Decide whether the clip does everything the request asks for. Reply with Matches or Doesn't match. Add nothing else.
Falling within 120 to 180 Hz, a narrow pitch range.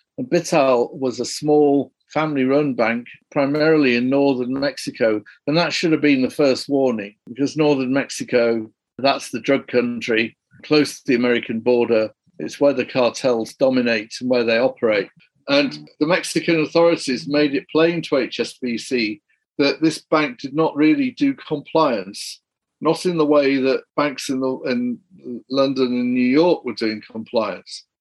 Doesn't match